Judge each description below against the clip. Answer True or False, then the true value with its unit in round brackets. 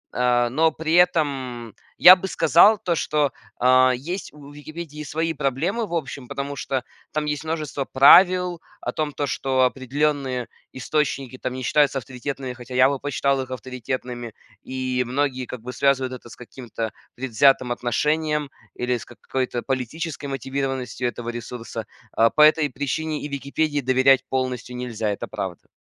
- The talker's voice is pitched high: False (135 Hz)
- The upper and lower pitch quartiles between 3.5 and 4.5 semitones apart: False (3.1 semitones)